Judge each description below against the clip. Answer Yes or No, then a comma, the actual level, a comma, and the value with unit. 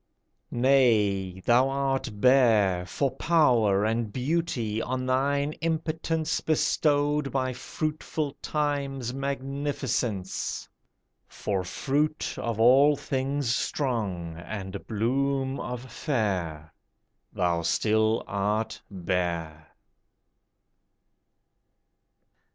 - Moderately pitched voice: No, low, 125 Hz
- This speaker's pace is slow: Yes, slow, 80 wpm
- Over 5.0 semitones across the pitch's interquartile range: Yes, wide, 5.4 semitones